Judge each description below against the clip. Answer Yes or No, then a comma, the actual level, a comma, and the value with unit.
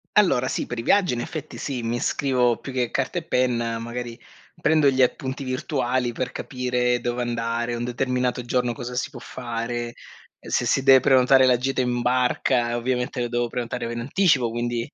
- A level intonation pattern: Yes, narrow, 1.5 semitones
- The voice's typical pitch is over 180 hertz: No, low, 125 Hz